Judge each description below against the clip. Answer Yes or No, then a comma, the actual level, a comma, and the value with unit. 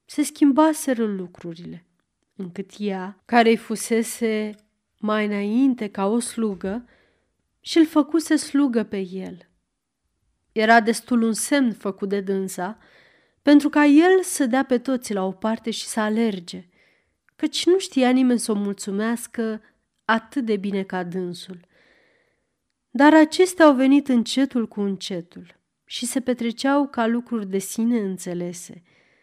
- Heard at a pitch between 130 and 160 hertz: No, high, 225 Hz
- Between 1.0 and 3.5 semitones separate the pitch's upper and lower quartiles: No, average, 5.2 semitones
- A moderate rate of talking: Yes, average, 135 wpm